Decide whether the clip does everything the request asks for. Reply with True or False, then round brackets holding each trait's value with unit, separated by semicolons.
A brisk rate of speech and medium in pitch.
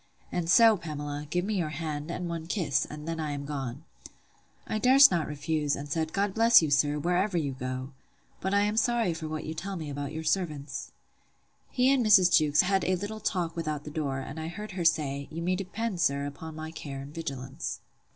True (210 wpm; 160 Hz)